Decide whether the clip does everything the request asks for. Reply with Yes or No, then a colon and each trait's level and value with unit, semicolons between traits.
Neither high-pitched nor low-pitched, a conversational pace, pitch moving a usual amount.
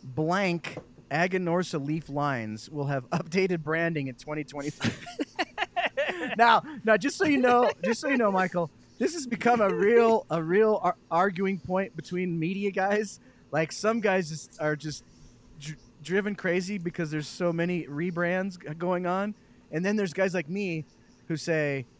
Yes: medium, 175 Hz; average, 160 wpm; average, 4.5 semitones